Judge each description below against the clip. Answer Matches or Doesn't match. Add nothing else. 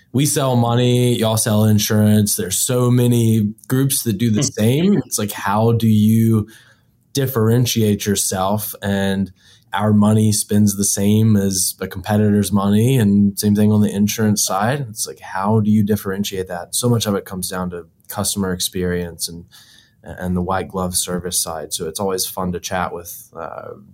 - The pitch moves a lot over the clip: Doesn't match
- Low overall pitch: Matches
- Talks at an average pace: Matches